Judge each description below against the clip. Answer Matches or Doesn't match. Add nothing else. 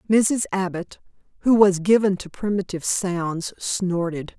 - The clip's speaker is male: Doesn't match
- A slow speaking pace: Matches